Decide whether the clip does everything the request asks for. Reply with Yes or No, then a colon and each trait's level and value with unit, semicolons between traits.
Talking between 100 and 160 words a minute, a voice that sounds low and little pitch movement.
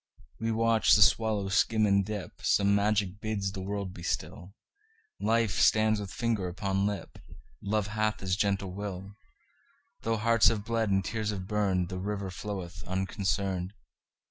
Yes: slow, 135 wpm; low, 100 Hz; narrow, 2.2 semitones